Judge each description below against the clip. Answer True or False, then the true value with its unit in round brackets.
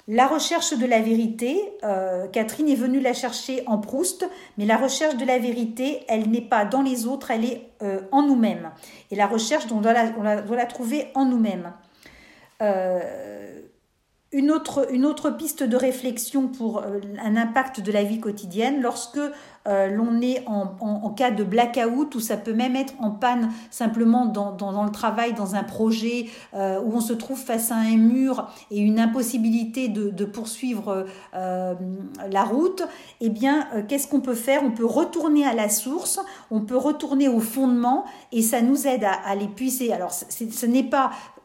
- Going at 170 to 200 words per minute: True (185 wpm)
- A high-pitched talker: True (235 Hz)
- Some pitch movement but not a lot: True (3.7 semitones)